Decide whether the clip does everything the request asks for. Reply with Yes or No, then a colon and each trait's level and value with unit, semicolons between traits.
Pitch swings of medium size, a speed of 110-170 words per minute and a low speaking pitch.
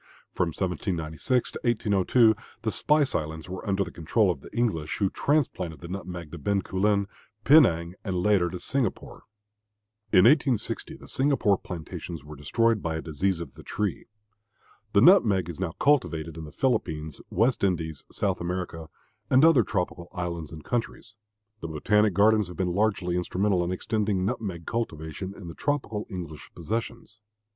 Yes: average, 4.7 semitones; average, 155 wpm; very low, 95 Hz